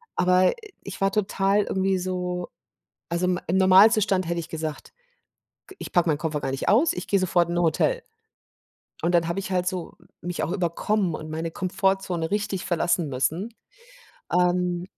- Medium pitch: Yes, medium, 180 Hz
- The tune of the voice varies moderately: No, narrow, 2.1 semitones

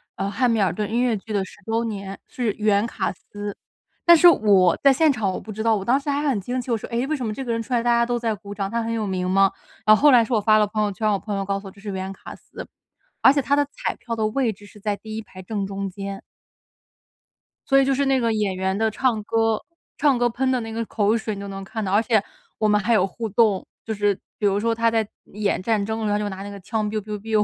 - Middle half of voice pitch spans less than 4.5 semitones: Yes, narrow, 2.6 semitones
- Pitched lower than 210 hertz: No, high, 215 Hz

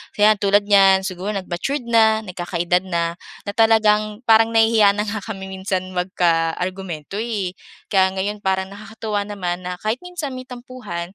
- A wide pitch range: No, average, 2.9 semitones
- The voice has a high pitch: Yes, high, 200 Hz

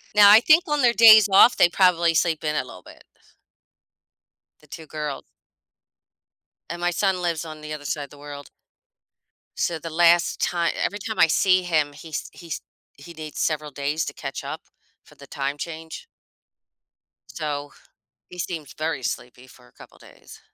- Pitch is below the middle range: No, medium, 160 Hz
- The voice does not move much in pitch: No, average, 3.2 semitones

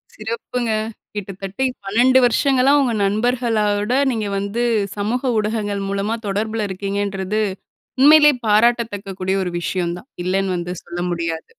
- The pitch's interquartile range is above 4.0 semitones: No, average, 3.4 semitones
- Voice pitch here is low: No, high, 210 Hz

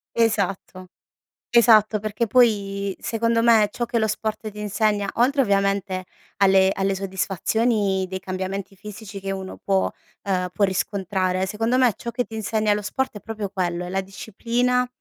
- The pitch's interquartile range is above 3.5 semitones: No, average, 2.8 semitones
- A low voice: No, high, 205 Hz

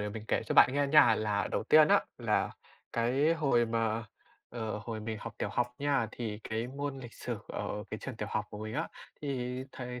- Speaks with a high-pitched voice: No, low, 115 Hz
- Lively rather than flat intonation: No, average, 3.8 semitones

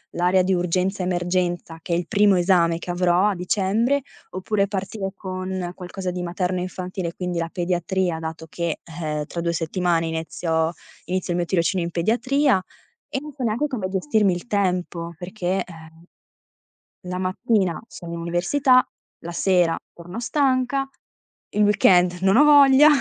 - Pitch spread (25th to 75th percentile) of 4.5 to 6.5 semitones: No, average, 2.7 semitones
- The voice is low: No, medium, 180 Hz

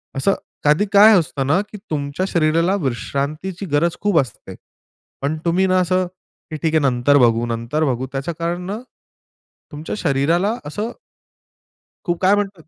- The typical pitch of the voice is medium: Yes, medium, 160 Hz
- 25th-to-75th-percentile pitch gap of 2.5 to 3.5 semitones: No, average, 4.8 semitones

